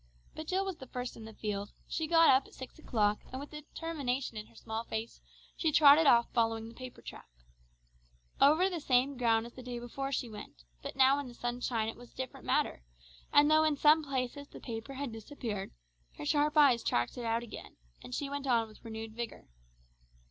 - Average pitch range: Yes, average, 4.1 semitones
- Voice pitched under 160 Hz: No, very high, 250 Hz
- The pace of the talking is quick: Yes, fast, 210 wpm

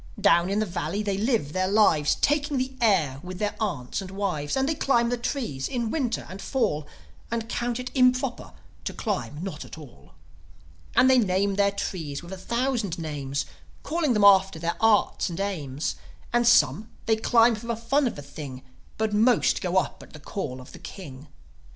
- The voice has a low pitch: No, high, 200 Hz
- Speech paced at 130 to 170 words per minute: No, average, 195 wpm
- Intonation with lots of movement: Yes, wide, 6.3 semitones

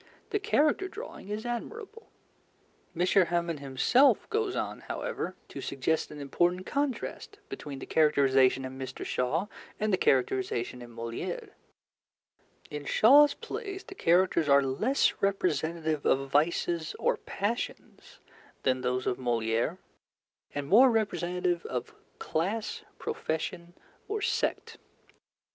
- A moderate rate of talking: No, slow, 120 wpm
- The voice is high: No, medium, 170 Hz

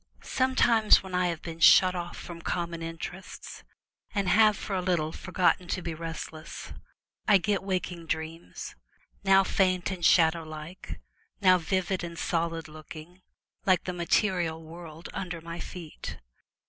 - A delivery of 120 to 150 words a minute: Yes, average, 145 wpm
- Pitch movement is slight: Yes, narrow, 2.3 semitones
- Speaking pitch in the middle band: Yes, medium, 175 Hz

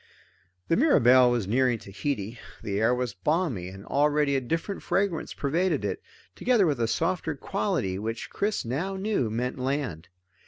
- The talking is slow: No, average, 155 wpm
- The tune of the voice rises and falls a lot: Yes, wide, 6.6 semitones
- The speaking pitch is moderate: No, low, 130 Hz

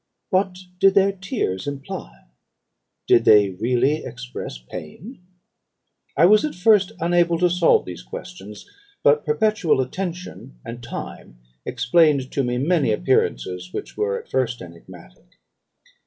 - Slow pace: Yes, slow, 125 wpm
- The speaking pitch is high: No, low, 135 Hz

